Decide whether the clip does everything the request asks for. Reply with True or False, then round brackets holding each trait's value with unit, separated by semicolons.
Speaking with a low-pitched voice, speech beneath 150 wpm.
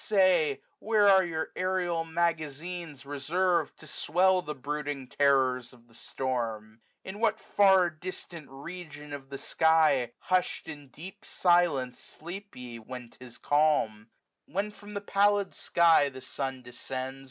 False (155 Hz; 140 wpm)